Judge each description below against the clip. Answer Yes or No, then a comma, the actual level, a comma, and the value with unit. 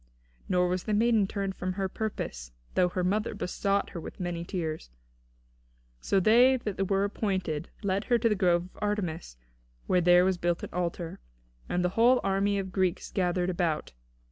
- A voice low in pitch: No, medium, 185 Hz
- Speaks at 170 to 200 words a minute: Yes, average, 180 wpm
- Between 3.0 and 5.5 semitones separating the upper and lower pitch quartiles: No, narrow, 2.4 semitones